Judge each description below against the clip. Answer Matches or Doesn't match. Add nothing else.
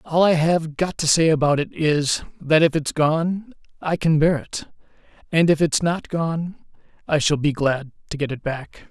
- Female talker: Doesn't match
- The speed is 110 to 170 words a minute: Doesn't match